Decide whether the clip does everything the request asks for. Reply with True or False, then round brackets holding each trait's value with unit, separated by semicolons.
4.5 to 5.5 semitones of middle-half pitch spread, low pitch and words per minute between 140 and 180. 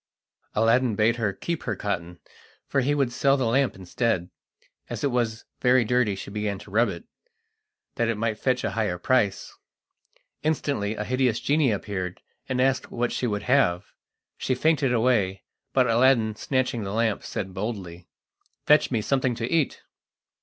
False (3.9 semitones; 115 Hz; 165 wpm)